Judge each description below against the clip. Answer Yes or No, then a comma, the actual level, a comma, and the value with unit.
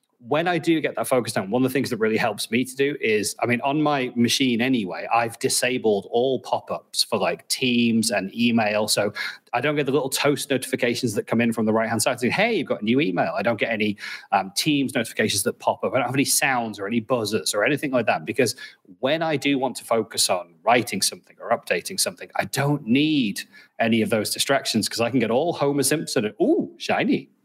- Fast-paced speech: Yes, fast, 235 wpm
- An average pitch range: Yes, average, 3.6 semitones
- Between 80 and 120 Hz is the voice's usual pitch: No, low, 130 Hz